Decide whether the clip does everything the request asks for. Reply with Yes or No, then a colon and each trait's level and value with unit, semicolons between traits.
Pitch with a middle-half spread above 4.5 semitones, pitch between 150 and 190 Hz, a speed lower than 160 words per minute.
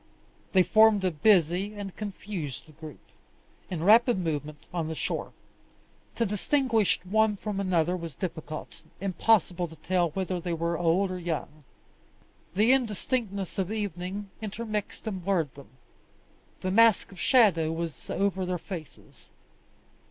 No: average, 3.8 semitones; medium, 185 Hz; slow, 135 wpm